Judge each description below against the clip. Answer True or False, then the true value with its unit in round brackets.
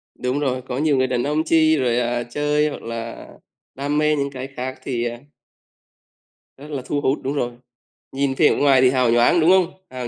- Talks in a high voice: False (135 Hz)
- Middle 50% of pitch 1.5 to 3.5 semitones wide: True (2.9 semitones)